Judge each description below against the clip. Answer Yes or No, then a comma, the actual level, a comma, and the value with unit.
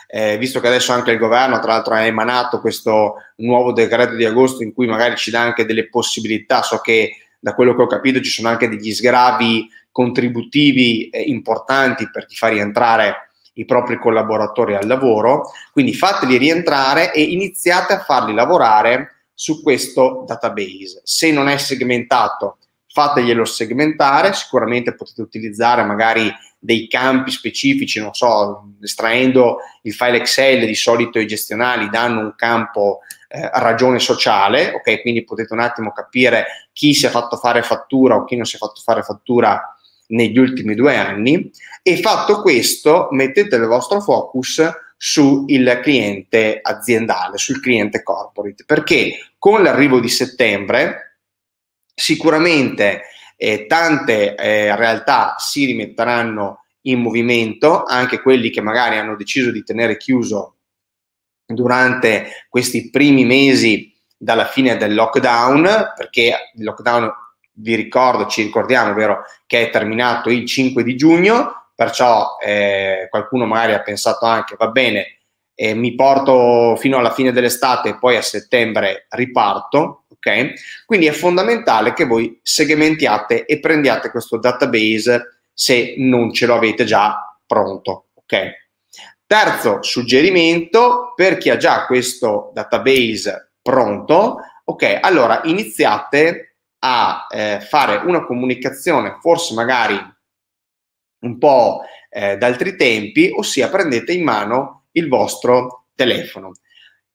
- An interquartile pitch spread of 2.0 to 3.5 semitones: Yes, average, 3.0 semitones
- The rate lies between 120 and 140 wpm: Yes, average, 135 wpm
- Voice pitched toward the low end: Yes, low, 120 Hz